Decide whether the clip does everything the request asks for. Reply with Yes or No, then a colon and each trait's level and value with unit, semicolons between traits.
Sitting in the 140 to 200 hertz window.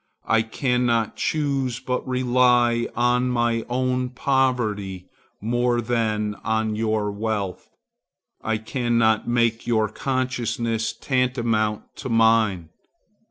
No: low, 115 Hz